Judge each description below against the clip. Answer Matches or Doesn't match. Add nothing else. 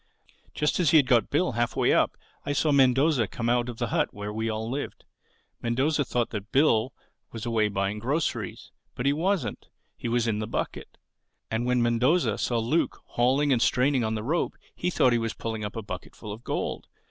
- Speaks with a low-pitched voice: Matches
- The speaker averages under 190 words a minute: Doesn't match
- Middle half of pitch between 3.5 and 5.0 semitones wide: Matches